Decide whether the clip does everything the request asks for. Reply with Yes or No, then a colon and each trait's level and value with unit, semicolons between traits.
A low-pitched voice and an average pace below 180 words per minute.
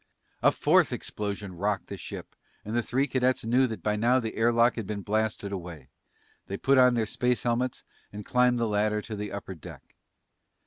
No: low, 110 Hz; average, 195 wpm